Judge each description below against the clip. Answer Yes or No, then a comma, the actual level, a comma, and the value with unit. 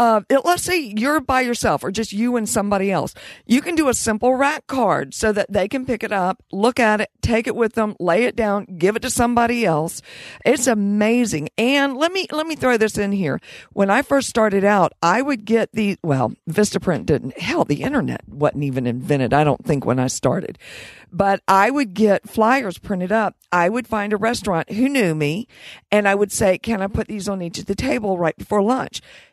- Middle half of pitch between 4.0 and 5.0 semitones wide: Yes, average, 4.5 semitones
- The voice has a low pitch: No, high, 210 Hz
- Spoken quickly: Yes, fast, 220 wpm